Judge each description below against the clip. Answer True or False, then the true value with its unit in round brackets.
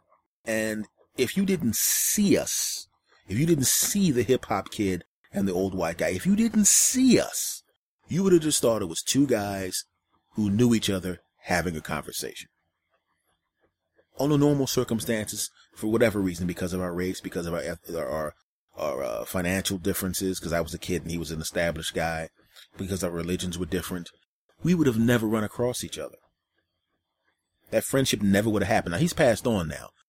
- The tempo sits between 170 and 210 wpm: True (185 wpm)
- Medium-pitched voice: False (100 Hz)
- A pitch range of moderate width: False (5.8 semitones)